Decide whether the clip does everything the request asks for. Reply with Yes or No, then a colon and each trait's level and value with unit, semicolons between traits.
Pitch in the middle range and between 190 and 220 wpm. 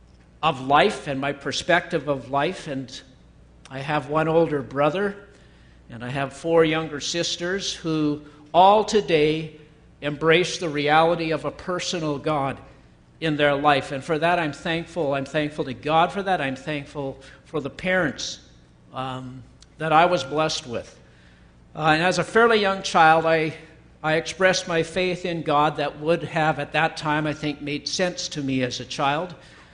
No: medium, 155 Hz; average, 165 wpm